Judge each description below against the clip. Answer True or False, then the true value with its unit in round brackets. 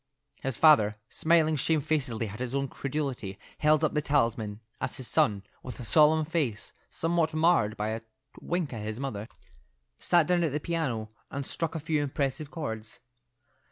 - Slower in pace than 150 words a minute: False (165 wpm)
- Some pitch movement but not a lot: False (5.7 semitones)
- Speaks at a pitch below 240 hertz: True (140 Hz)